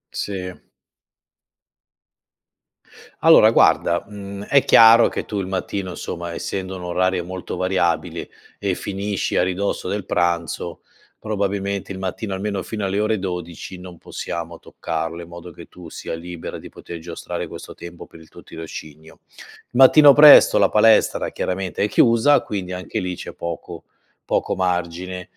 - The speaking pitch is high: No, very low, 95 Hz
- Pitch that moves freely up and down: No, average, 2.7 semitones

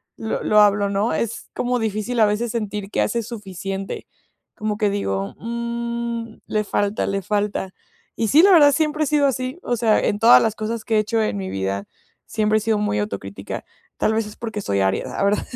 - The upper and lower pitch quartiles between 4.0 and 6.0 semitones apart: No, average, 2.7 semitones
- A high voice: Yes, high, 215 Hz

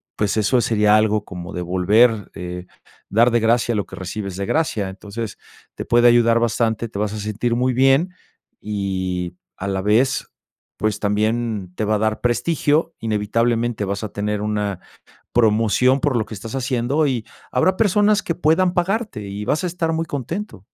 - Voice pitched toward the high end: No, low, 110 Hz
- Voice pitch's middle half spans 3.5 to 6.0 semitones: Yes, average, 3.8 semitones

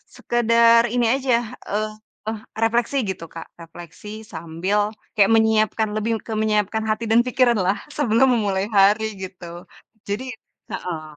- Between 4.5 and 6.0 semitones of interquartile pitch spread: No, average, 2.9 semitones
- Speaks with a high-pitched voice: Yes, high, 215 Hz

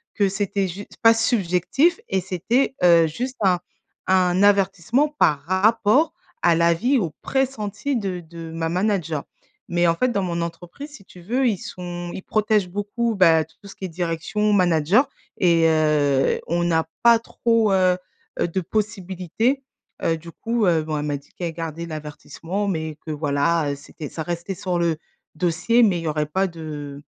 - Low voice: No, medium, 180 Hz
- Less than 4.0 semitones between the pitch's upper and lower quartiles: No, average, 4.3 semitones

